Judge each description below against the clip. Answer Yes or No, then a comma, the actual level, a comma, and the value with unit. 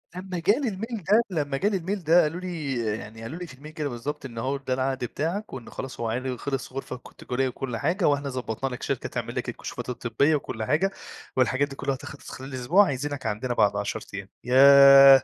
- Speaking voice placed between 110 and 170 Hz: Yes, low, 135 Hz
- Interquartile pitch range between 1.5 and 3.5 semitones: No, average, 4.3 semitones